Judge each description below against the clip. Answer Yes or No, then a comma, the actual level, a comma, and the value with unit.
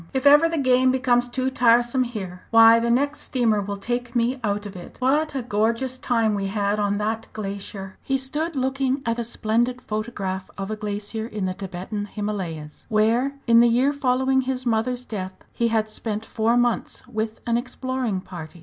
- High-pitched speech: Yes, high, 230 Hz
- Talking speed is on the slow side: No, average, 185 wpm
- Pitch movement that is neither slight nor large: Yes, average, 3.6 semitones